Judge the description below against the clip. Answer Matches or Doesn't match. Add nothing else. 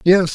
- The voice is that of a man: Matches